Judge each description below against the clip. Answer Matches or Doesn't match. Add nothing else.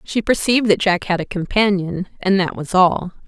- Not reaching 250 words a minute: Matches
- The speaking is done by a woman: Matches